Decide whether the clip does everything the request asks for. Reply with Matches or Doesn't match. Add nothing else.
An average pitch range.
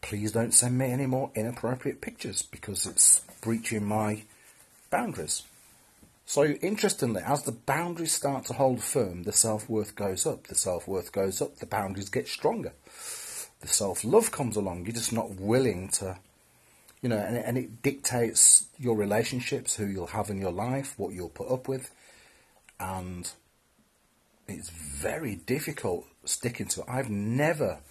Matches